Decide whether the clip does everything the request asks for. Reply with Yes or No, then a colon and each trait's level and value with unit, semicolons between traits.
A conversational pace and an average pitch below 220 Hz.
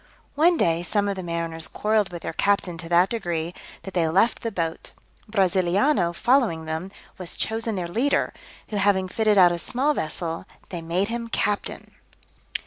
Yes: average, 170 wpm; medium, 185 Hz